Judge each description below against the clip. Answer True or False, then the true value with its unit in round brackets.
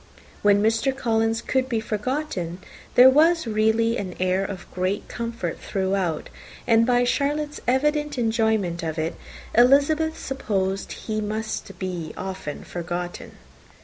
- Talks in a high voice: True (220 Hz)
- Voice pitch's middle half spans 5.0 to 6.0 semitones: True (5.5 semitones)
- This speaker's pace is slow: True (125 wpm)